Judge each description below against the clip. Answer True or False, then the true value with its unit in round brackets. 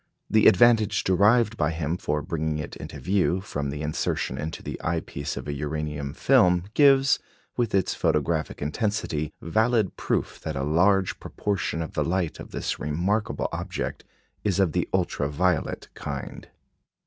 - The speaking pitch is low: True (85 Hz)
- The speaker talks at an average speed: True (160 wpm)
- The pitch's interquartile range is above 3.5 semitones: True (5.2 semitones)